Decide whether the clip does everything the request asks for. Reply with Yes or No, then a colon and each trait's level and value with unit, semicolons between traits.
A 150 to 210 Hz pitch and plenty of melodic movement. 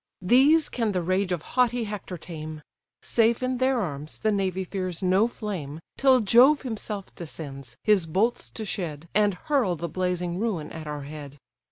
Yes: high, 190 Hz; wide, 5.9 semitones